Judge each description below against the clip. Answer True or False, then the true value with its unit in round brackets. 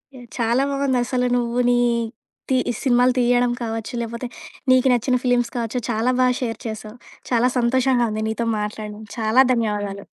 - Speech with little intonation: True (2.1 semitones)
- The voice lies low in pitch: False (240 Hz)